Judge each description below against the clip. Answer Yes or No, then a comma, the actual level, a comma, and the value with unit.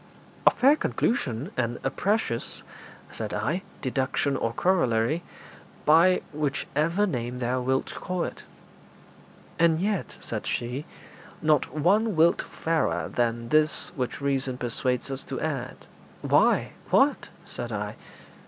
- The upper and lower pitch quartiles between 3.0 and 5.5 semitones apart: Yes, average, 5.1 semitones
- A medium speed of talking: No, slow, 125 wpm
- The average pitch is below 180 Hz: Yes, medium, 140 Hz